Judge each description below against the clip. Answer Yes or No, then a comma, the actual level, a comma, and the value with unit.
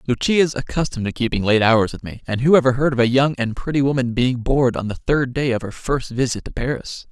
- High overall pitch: No, low, 125 Hz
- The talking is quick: Yes, fast, 255 wpm